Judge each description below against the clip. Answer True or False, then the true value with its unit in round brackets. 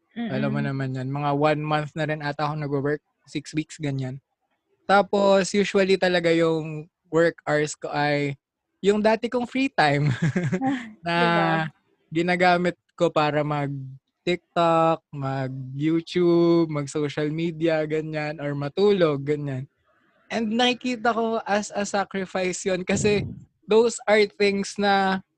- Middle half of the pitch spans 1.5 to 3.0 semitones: False (4.8 semitones)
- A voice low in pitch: False (165 Hz)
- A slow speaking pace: True (125 wpm)